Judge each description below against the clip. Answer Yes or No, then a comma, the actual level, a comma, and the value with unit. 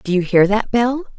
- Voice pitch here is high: Yes, high, 215 Hz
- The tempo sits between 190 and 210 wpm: No, fast, 255 wpm